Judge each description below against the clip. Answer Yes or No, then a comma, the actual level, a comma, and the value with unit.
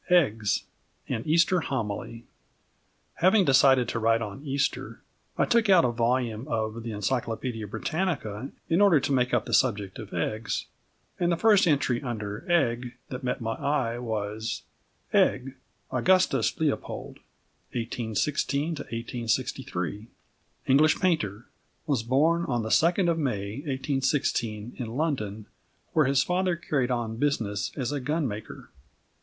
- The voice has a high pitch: No, low, 125 Hz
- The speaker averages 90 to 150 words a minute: Yes, average, 140 wpm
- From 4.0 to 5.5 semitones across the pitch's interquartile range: Yes, average, 5.1 semitones